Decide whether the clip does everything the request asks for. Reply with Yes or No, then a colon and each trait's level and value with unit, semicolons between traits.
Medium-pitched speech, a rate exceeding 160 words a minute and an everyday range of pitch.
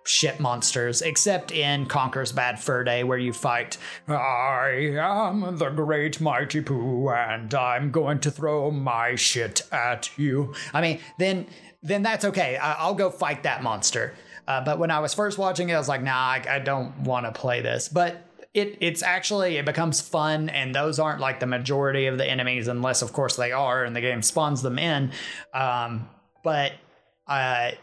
Yes: medium, 145 Hz; average, 185 wpm; average, 4.2 semitones